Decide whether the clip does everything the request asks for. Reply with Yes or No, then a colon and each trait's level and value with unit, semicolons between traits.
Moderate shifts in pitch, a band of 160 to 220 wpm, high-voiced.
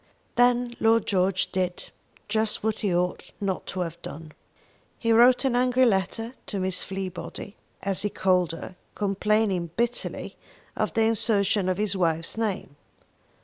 No: average, 3.6 semitones; average, 145 wpm; high, 200 Hz